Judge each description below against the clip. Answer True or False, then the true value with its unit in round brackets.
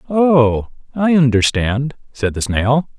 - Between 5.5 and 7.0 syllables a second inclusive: False (3.5 syllables/s)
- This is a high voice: False (130 Hz)